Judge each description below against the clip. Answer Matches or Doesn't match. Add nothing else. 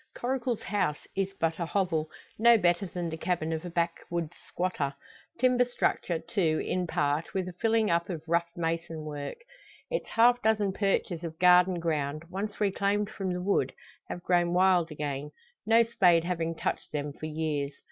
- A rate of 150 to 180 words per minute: Matches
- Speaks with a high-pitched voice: Doesn't match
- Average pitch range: Matches